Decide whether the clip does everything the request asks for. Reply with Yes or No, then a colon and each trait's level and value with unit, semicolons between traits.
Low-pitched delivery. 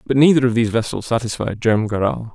Yes: low, 115 Hz